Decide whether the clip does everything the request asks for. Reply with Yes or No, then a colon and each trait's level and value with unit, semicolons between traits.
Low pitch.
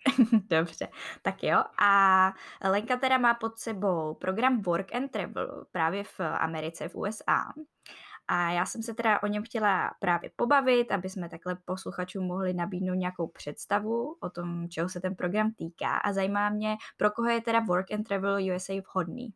No: high, 195 Hz